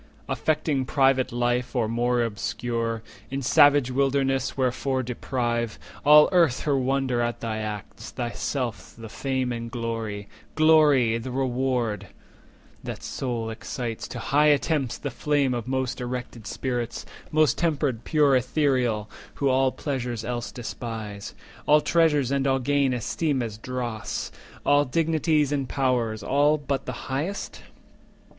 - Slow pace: Yes, slow, 130 wpm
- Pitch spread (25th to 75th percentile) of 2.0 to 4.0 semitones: Yes, average, 3.1 semitones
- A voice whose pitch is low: Yes, low, 130 Hz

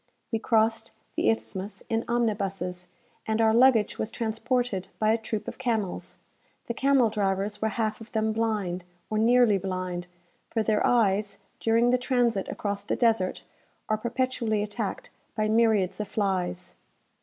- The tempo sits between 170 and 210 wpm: No, average, 150 wpm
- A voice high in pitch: Yes, high, 220 Hz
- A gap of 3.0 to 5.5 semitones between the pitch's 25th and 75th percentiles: No, narrow, 2.6 semitones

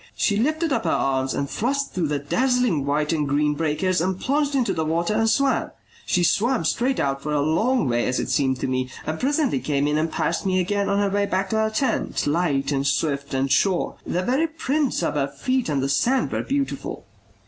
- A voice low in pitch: No, medium, 180 Hz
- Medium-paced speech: No, fast, 225 wpm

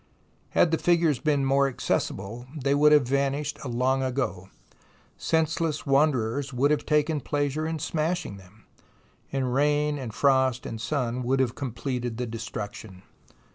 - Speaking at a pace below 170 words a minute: Yes, average, 140 wpm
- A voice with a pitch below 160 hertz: Yes, low, 135 Hz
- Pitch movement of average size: Yes, average, 3.4 semitones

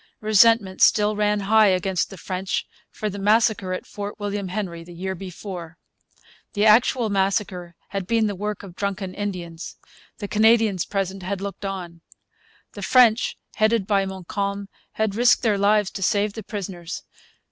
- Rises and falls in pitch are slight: Yes, narrow, 2.1 semitones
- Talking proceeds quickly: No, average, 160 wpm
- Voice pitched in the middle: No, high, 200 Hz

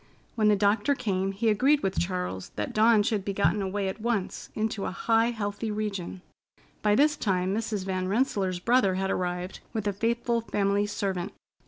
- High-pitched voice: Yes, high, 205 Hz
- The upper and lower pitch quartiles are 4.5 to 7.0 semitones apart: No, average, 2.9 semitones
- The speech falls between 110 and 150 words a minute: No, average, 180 wpm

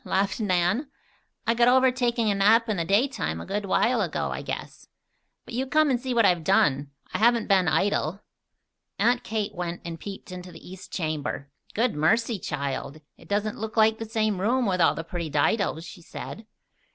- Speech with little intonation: No, average, 4.9 semitones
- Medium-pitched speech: No, high, 205 Hz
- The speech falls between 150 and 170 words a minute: No, average, 200 wpm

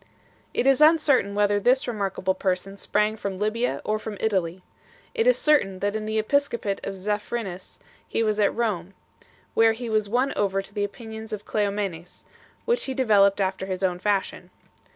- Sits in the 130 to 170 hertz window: No, high, 210 Hz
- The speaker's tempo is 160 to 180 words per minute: Yes, average, 175 wpm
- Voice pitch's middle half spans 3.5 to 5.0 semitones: No, average, 2.7 semitones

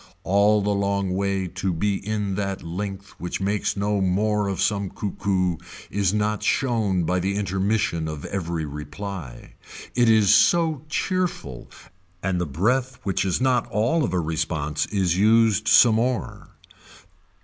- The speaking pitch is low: Yes, low, 100 Hz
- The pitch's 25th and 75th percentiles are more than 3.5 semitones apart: No, average, 2.8 semitones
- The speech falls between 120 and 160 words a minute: Yes, average, 150 wpm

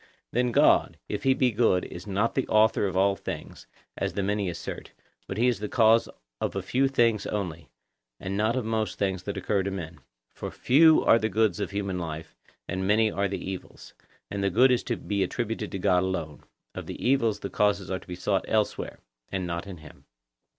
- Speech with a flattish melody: No, average, 3.1 semitones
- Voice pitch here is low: Yes, low, 100 Hz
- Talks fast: Yes, fast, 215 wpm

